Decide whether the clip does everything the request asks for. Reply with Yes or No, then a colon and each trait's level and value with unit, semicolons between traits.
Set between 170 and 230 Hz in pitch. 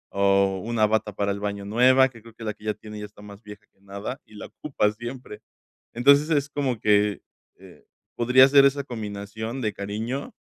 No: low, 110 Hz